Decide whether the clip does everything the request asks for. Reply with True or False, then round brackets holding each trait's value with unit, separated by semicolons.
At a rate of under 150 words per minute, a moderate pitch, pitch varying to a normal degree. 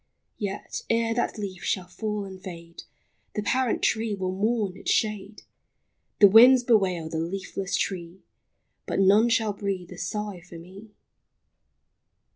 False (140 wpm; 200 Hz; 3.0 semitones)